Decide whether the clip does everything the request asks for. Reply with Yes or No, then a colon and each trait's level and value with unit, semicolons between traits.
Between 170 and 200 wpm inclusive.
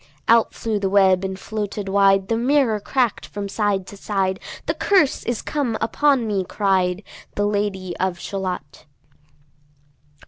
No: average, 145 wpm